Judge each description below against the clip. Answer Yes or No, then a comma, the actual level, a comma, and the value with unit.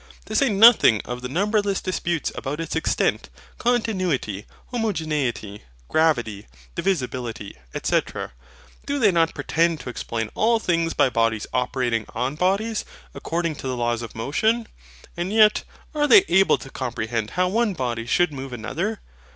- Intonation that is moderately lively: No, wide, 8.7 semitones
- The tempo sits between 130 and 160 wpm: Yes, average, 145 wpm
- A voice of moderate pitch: Yes, medium, 160 Hz